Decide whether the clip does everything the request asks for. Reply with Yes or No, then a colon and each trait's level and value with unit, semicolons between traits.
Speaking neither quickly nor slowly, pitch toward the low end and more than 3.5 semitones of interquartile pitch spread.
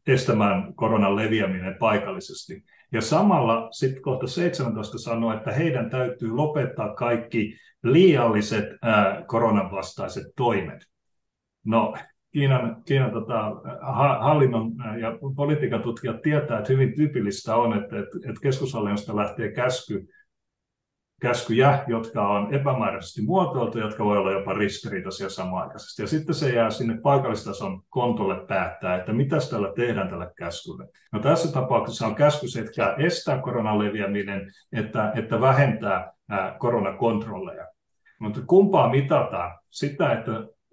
Yes: average, 120 wpm; low, 115 Hz; average, 4.4 semitones